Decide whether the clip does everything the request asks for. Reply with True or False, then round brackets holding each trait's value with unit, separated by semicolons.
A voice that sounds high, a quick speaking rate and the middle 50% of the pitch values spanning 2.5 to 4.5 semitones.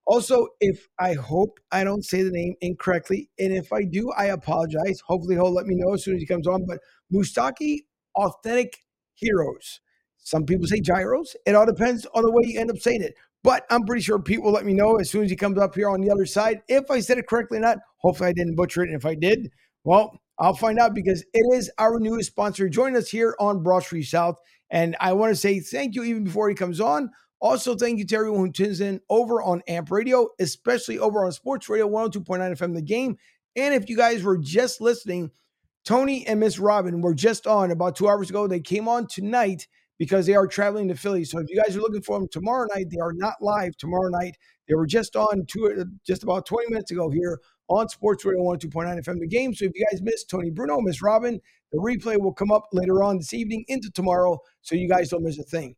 True (200 Hz; 235 wpm; 3.9 semitones)